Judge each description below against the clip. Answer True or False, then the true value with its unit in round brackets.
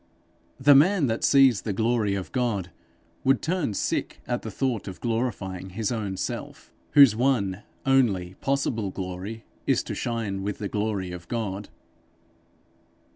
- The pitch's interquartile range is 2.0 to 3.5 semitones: False (4.6 semitones)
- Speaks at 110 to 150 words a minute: True (145 wpm)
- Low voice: True (110 Hz)